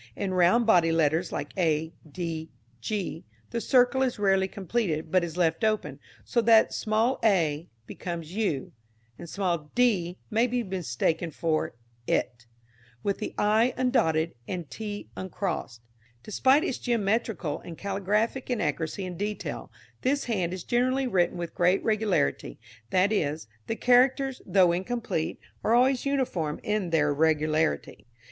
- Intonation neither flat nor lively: No, wide, 5.7 semitones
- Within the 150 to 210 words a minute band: No, average, 140 wpm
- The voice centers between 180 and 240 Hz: Yes, high, 190 Hz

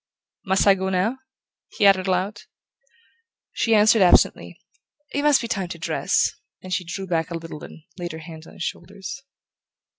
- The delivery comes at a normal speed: Yes, average, 175 wpm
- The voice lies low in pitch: No, high, 190 Hz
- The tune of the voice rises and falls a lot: No, average, 3.0 semitones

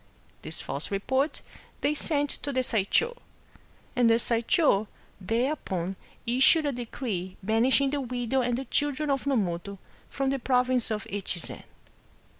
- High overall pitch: Yes, high, 245 Hz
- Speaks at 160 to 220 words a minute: No, average, 140 wpm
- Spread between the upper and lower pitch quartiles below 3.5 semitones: No, average, 4.6 semitones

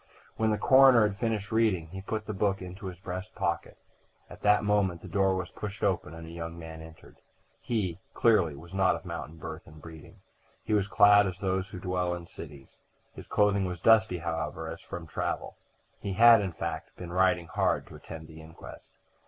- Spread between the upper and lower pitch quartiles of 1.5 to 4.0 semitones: Yes, average, 3.7 semitones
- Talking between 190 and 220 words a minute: Yes, average, 200 wpm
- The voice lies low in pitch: Yes, very low, 95 Hz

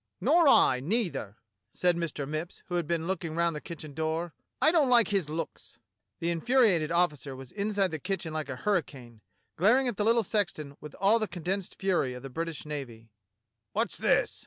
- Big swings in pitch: No, average, 4.8 semitones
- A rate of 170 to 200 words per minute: Yes, average, 190 wpm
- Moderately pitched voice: Yes, medium, 170 Hz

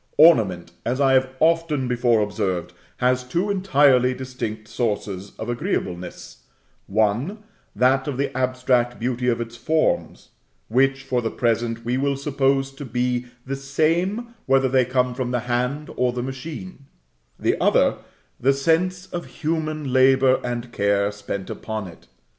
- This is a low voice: Yes, low, 130 Hz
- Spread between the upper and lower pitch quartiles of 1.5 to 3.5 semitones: Yes, average, 2.9 semitones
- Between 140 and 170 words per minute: Yes, average, 145 wpm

